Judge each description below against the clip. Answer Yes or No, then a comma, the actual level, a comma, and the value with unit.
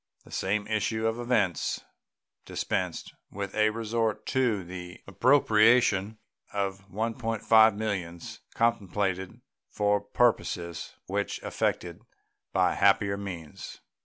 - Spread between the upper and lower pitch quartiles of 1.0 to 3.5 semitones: Yes, average, 2.8 semitones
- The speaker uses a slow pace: Yes, slow, 105 wpm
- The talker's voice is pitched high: No, low, 105 Hz